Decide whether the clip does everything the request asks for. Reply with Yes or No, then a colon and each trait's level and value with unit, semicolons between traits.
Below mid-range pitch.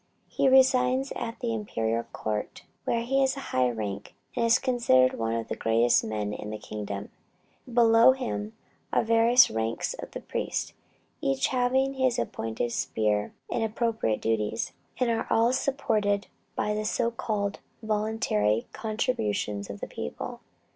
No: high, 215 Hz